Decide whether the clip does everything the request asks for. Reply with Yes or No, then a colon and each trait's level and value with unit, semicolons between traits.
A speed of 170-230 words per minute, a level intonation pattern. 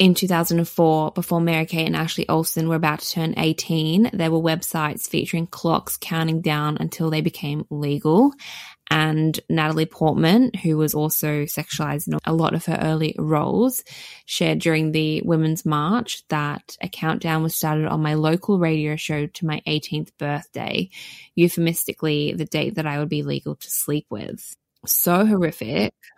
No: average, 160 wpm; narrow, 1.8 semitones